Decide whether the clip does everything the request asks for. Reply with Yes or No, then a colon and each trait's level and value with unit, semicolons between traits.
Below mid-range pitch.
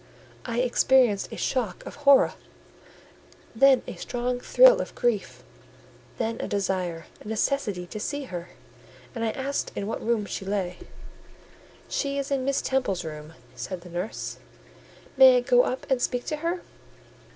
No: high, 240 Hz